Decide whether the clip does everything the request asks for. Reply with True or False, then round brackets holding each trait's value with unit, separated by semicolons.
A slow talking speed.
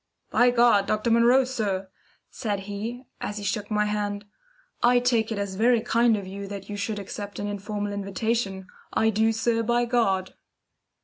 False (175 wpm)